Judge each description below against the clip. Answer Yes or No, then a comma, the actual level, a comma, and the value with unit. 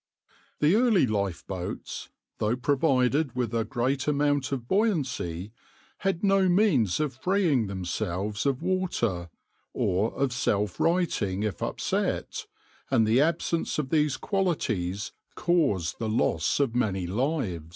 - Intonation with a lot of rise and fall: Yes, wide, 7.5 semitones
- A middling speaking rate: No, slow, 125 wpm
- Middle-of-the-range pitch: No, low, 130 Hz